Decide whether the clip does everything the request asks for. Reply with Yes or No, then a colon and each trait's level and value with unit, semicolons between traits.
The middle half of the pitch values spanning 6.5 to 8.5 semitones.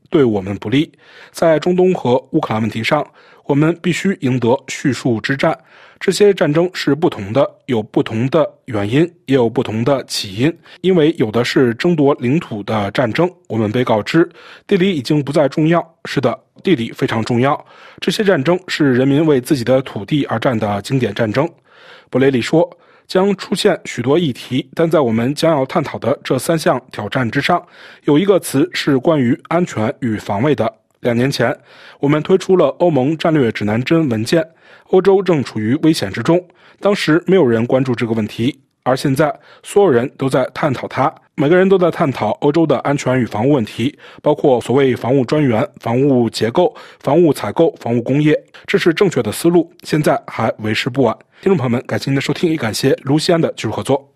No: wide, 5.7 semitones